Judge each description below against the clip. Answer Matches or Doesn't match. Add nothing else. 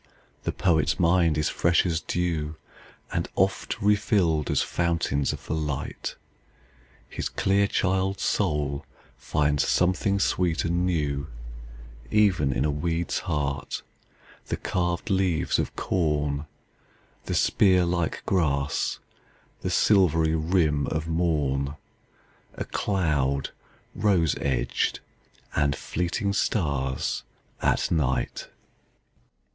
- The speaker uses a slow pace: Matches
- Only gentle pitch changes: Doesn't match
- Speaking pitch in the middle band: Doesn't match